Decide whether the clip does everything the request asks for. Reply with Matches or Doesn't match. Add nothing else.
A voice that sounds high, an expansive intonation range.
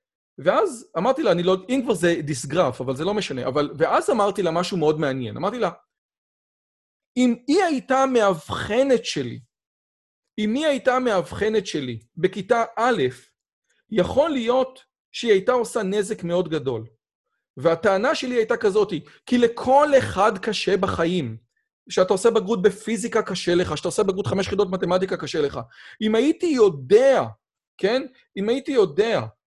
Matches